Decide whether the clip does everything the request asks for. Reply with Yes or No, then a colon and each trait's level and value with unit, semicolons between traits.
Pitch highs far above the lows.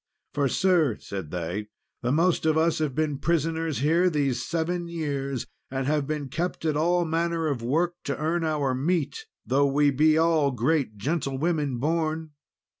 No: average, 3.3 semitones